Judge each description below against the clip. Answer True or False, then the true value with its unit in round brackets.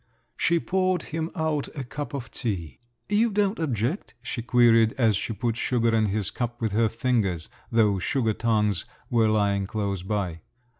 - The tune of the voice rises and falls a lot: False (4.8 semitones)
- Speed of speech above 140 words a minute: True (165 wpm)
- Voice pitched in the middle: False (115 Hz)